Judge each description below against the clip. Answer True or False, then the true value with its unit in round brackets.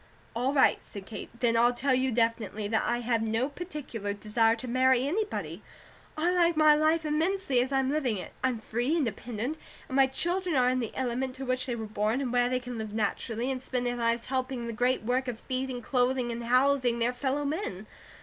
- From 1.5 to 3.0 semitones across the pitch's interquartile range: True (2.7 semitones)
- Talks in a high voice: True (250 Hz)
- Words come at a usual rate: False (215 wpm)